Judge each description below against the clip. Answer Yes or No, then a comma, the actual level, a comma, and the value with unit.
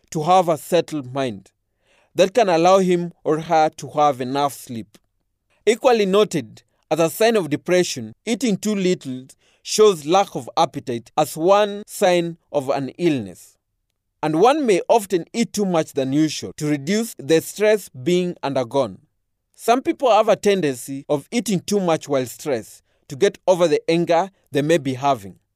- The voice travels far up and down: Yes, wide, 5.8 semitones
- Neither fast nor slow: Yes, average, 165 wpm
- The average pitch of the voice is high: No, medium, 160 Hz